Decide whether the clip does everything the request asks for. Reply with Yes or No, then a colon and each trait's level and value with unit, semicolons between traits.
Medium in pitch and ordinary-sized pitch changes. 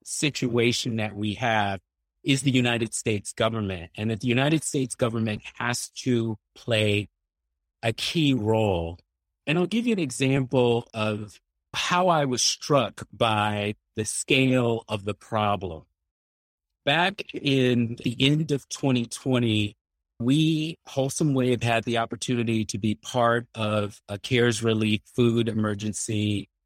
No: low, 115 Hz; average, 3.5 semitones